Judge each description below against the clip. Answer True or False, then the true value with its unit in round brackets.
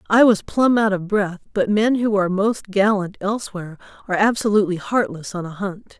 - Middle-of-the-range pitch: False (200 Hz)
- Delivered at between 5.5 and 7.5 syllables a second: True (5.6 syllables/s)